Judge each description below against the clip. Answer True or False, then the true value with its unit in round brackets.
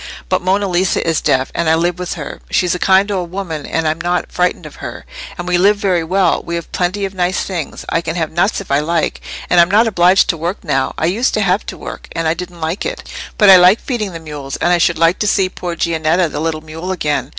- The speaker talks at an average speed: False (260 wpm)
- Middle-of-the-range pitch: True (175 Hz)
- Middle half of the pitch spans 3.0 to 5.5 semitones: False (2.5 semitones)